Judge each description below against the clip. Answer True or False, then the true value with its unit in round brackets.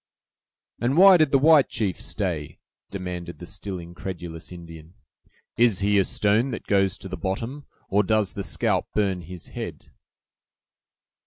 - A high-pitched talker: False (95 Hz)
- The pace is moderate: True (150 wpm)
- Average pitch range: True (4.2 semitones)